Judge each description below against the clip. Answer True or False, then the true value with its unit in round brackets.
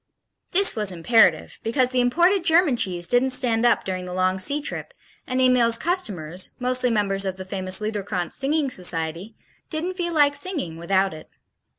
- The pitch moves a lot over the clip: True (7.1 semitones)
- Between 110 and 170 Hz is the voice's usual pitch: False (230 Hz)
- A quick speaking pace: False (170 wpm)